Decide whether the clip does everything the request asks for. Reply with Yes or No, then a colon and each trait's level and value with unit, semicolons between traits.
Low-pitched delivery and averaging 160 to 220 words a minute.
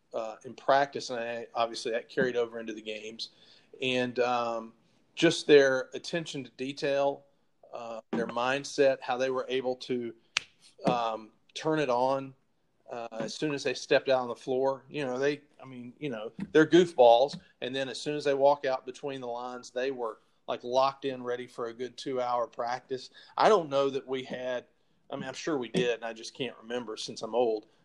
Yes: low, 130 Hz; average, 200 wpm